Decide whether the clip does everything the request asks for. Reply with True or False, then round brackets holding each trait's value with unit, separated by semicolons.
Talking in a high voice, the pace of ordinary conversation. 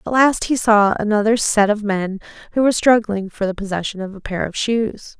False (210 Hz; 220 wpm)